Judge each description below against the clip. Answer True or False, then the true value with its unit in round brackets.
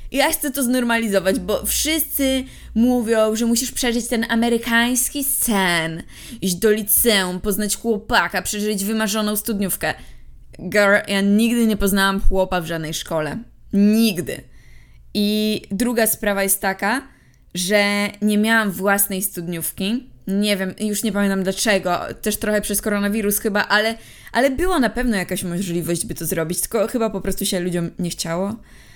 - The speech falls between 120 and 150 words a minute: True (145 wpm)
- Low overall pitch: False (210 Hz)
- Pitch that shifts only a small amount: False (3.1 semitones)